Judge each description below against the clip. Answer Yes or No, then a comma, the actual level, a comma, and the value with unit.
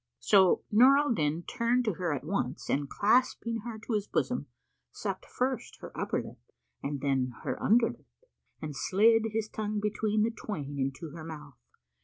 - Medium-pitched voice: No, high, 205 Hz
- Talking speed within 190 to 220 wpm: No, average, 175 wpm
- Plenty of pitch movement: Yes, wide, 7.4 semitones